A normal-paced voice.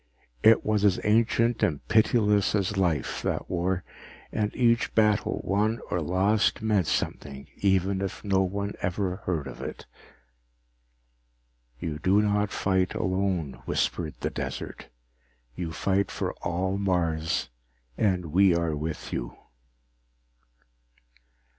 No: slow, 120 wpm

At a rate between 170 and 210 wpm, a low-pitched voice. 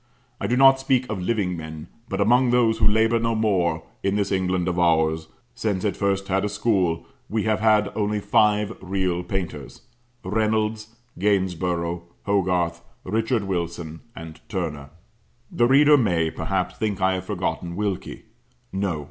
No: average, 155 wpm; low, 100 Hz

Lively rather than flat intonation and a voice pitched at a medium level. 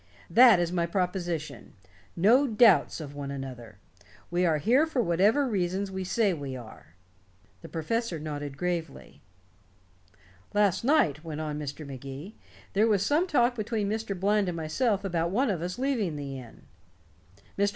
Yes: wide, 6.1 semitones; medium, 180 Hz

